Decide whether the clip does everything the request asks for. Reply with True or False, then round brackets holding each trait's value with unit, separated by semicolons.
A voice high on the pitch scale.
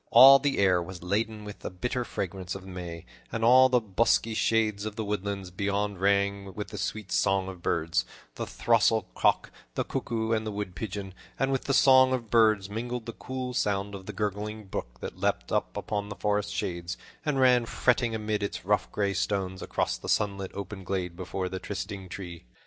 False (100 Hz)